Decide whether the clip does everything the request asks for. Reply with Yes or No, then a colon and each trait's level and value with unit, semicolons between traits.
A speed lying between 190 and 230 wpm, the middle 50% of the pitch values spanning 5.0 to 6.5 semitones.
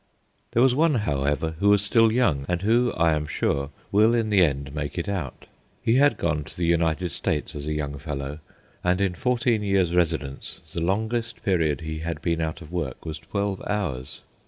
Yes: average, 200 wpm; wide, 5.5 semitones